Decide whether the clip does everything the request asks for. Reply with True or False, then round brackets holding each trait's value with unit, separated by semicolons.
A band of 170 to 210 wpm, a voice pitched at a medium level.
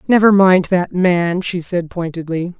False (160 wpm; 180 Hz)